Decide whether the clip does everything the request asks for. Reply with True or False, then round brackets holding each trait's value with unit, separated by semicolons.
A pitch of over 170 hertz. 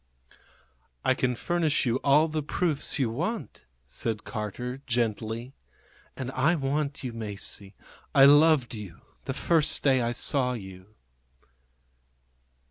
False (130 Hz)